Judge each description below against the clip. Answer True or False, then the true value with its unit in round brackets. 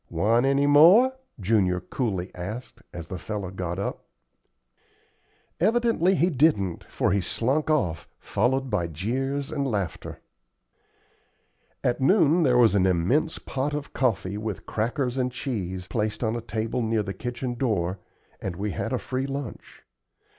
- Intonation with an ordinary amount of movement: False (6.1 semitones)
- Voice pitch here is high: False (115 Hz)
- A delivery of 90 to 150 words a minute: True (145 wpm)